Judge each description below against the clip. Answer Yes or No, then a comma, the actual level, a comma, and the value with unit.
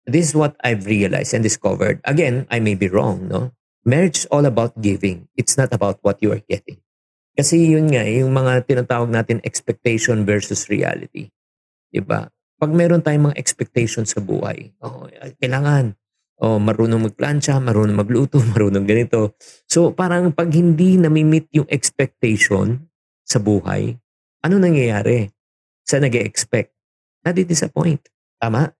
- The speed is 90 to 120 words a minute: No, average, 140 wpm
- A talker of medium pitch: No, low, 125 Hz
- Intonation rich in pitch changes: Yes, wide, 5.9 semitones